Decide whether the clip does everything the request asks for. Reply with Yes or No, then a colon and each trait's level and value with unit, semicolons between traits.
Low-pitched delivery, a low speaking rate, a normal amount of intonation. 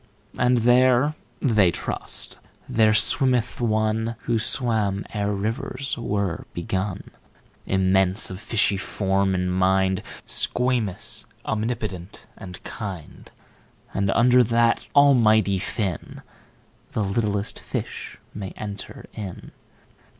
Yes: low, 105 Hz; slow, 85 wpm; average, 3.5 semitones